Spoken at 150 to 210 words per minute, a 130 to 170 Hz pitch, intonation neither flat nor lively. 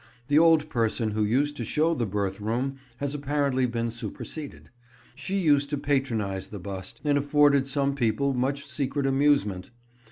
Yes: average, 160 wpm; low, 135 Hz; average, 4.1 semitones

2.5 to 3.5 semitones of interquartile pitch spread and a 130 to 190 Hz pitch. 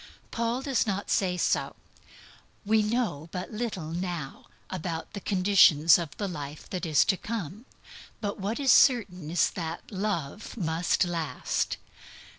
No: average, 4.4 semitones; medium, 185 Hz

